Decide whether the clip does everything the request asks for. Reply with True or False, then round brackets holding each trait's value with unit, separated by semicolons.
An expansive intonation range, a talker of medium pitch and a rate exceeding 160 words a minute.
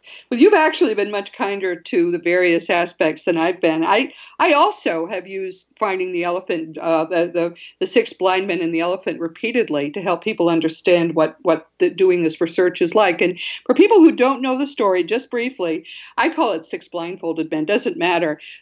True (6.8 semitones; 180 Hz; 200 wpm)